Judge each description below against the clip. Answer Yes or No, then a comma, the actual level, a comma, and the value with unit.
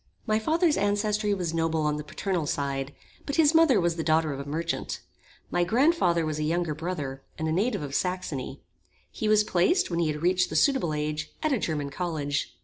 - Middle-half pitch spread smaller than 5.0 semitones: No, wide, 5.6 semitones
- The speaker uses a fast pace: Yes, fast, 210 wpm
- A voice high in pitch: No, medium, 170 Hz